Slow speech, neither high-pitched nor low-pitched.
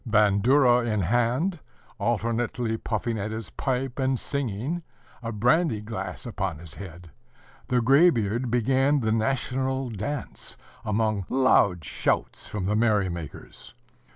No: slow, 125 wpm; low, 115 Hz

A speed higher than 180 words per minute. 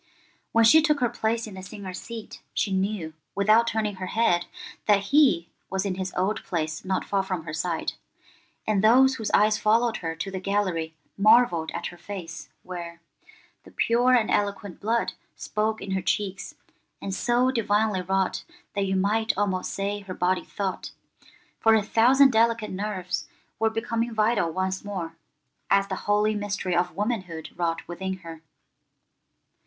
No: average, 165 wpm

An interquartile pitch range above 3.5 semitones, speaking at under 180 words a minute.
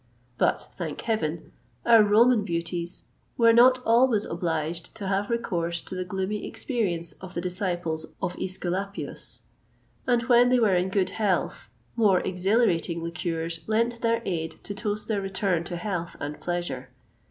Yes: average, 4.5 semitones; average, 150 wpm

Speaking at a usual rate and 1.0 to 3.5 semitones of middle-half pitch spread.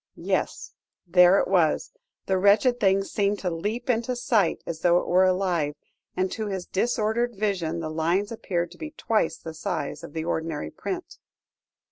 No: average, 170 wpm; average, 4.1 semitones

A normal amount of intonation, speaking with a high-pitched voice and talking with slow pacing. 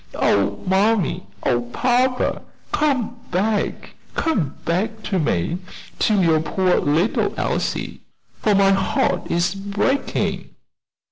Yes: average, 4.8 semitones; high, 195 Hz; slow, 110 wpm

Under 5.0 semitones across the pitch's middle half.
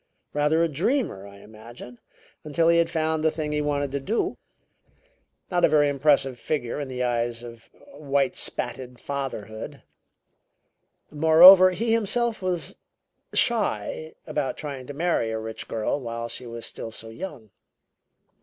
No: wide, 5.6 semitones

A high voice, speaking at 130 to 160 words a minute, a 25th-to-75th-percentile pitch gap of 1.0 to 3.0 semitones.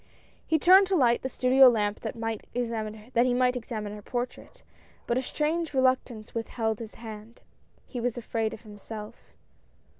Yes: high, 235 Hz; average, 150 wpm; average, 2.7 semitones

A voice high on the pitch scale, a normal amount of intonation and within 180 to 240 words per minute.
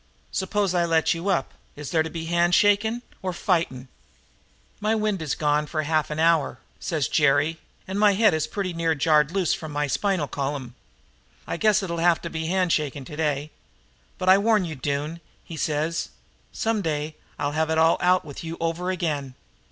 No: medium, 165 Hz; average, 3.7 semitones; average, 185 wpm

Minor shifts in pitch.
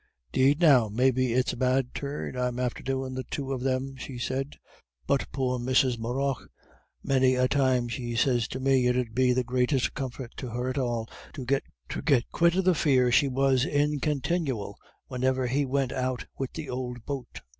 Yes: narrow, 1.6 semitones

